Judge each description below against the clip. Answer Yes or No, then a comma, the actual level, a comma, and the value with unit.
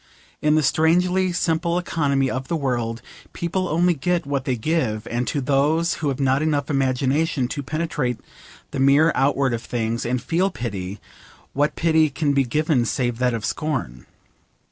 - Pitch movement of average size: Yes, average, 4.2 semitones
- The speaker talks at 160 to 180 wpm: Yes, average, 165 wpm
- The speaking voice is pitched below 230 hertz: Yes, medium, 140 Hz